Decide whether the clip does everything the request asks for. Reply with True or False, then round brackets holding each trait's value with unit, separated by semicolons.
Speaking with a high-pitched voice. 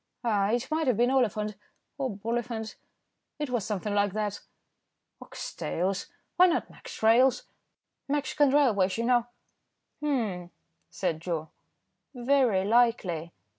True (230 Hz)